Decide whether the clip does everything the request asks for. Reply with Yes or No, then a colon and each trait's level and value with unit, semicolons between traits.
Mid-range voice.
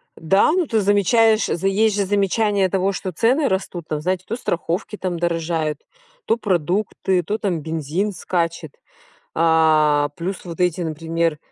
Yes: medium, 180 Hz